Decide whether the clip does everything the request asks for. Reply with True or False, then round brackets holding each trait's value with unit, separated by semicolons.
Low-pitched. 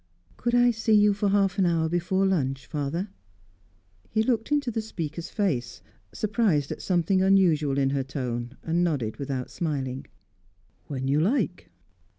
False (170 Hz)